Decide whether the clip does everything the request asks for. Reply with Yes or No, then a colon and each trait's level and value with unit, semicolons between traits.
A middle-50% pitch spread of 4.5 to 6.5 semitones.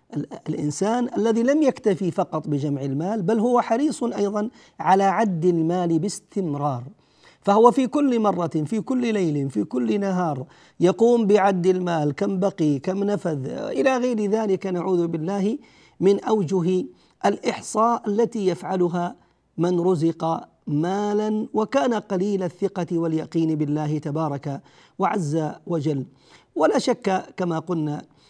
Yes: average, 5.0 semitones